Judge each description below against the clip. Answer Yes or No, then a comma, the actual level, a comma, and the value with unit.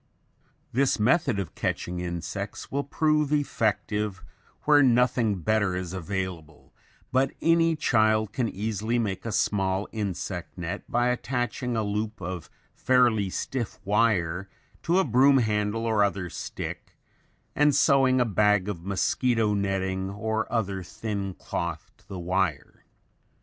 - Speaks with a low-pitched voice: Yes, low, 105 Hz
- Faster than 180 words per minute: No, slow, 135 wpm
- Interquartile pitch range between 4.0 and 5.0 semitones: Yes, average, 4.3 semitones